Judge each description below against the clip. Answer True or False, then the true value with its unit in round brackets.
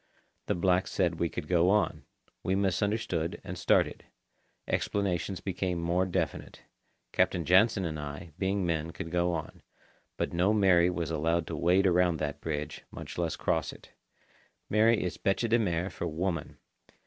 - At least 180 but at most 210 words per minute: False (160 wpm)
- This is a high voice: False (90 Hz)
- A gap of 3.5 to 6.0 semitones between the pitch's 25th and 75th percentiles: False (2.5 semitones)